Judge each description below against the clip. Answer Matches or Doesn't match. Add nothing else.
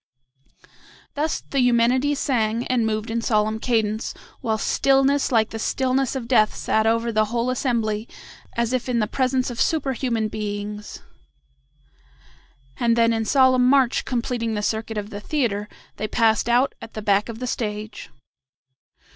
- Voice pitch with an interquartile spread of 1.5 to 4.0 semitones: Matches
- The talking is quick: Doesn't match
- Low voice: Doesn't match